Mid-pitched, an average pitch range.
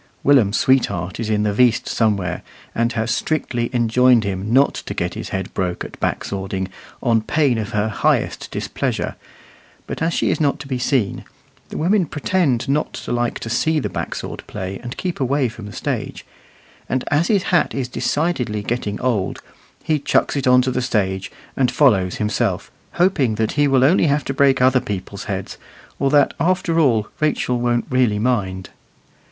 No: low, 125 Hz; average, 5.0 semitones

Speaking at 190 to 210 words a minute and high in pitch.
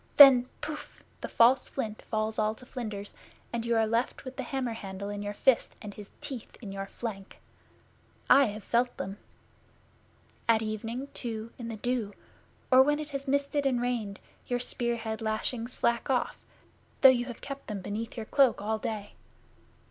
No: average, 180 wpm; high, 230 Hz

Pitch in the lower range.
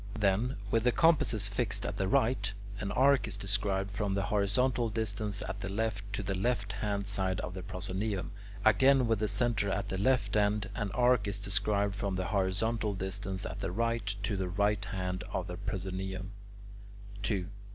Yes: low, 100 Hz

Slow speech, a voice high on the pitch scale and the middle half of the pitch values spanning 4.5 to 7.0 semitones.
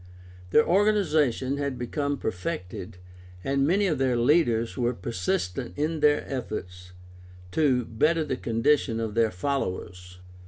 No: slow, 125 wpm; low, 130 Hz; average, 5.1 semitones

